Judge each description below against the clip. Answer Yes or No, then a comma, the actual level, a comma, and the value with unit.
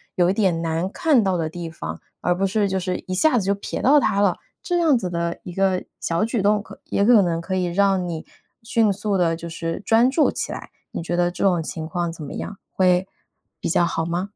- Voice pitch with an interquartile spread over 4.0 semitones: No, average, 3.2 semitones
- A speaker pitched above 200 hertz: No, medium, 185 Hz